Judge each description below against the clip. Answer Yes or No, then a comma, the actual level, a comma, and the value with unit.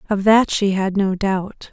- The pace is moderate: No, fast, 210 wpm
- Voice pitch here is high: Yes, high, 200 Hz